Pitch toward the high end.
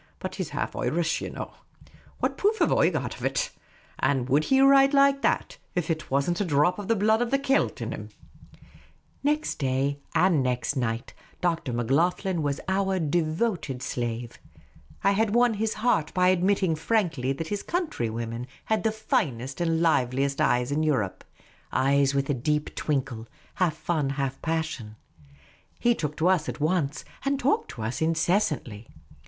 No: medium, 160 Hz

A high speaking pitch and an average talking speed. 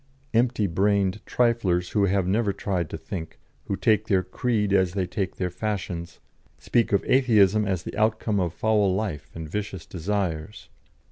No: low, 100 Hz; average, 160 wpm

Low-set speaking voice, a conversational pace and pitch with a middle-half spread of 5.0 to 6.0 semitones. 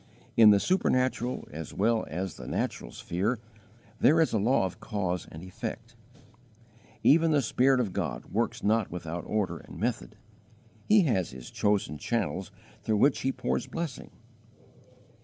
Yes: low, 110 Hz; average, 150 wpm; wide, 5.5 semitones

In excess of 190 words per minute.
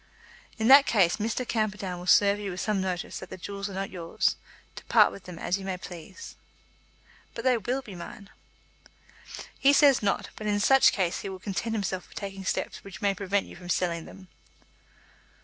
Yes: average, 200 wpm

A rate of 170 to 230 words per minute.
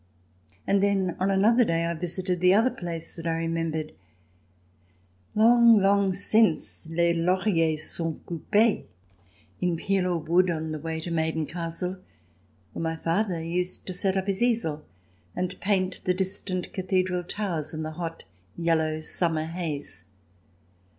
No: average, 150 wpm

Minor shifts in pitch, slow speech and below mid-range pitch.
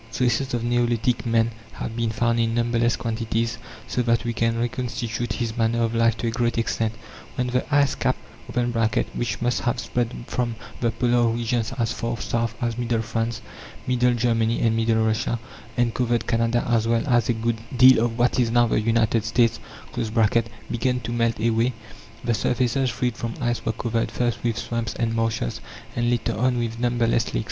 No: narrow, 1.0 semitones; average, 185 wpm; low, 115 Hz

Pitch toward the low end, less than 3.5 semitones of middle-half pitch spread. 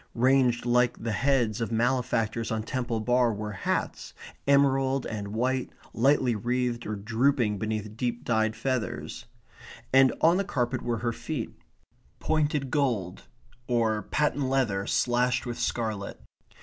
Yes: low, 120 Hz; average, 3.0 semitones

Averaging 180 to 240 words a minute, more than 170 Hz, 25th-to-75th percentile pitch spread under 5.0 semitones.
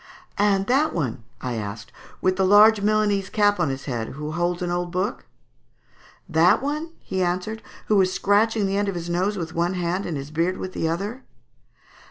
Yes: average, 195 wpm; medium, 185 Hz; average, 3.4 semitones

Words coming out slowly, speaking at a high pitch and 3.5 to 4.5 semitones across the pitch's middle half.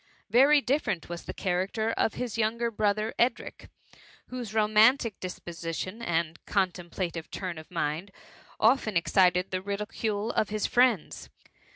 Yes: slow, 130 wpm; high, 205 Hz; average, 4.2 semitones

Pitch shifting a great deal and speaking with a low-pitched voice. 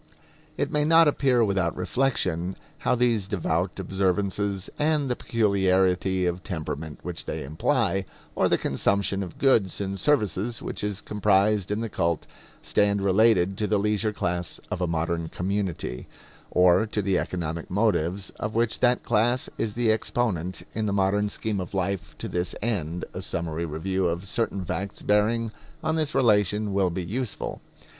No: average, 3.4 semitones; low, 100 Hz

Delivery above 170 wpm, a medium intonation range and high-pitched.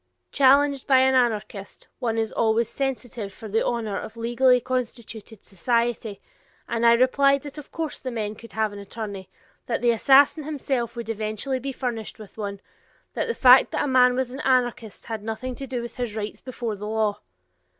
Yes: average, 190 wpm; average, 3.0 semitones; high, 235 Hz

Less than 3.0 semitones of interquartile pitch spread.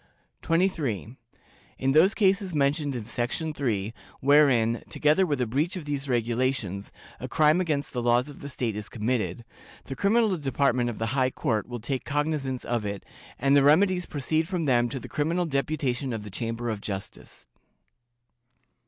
No: average, 4.4 semitones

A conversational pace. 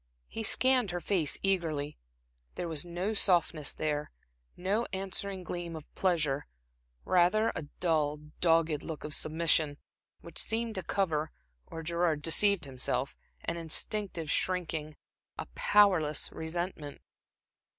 No: slow, 120 wpm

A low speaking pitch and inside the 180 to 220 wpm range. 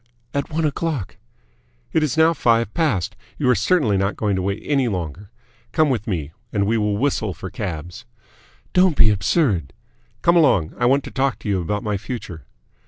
Yes: low, 110 Hz; average, 185 wpm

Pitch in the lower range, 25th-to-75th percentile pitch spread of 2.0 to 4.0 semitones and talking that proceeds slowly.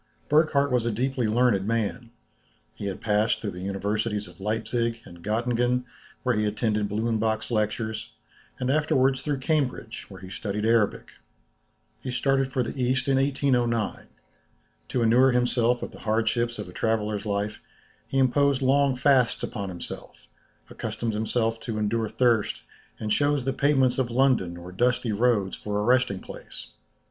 No: low, 115 Hz; average, 3.3 semitones; average, 155 wpm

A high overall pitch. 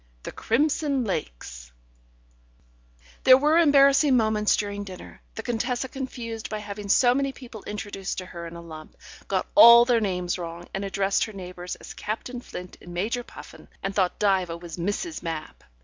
Yes: high, 210 Hz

